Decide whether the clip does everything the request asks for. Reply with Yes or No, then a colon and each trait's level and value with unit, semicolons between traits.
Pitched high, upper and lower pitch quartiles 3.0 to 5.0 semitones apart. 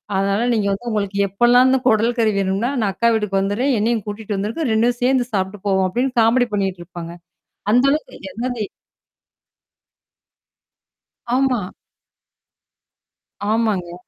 Yes: high, 215 Hz; average, 3.6 semitones